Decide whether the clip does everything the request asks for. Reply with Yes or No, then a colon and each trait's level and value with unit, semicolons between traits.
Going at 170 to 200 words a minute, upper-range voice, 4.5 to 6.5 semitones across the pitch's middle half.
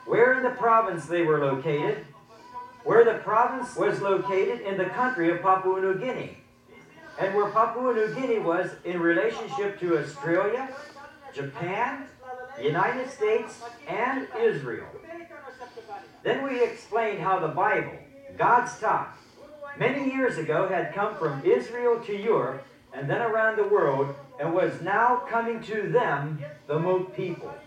No: average, 140 wpm; high, 225 Hz; wide, 5.6 semitones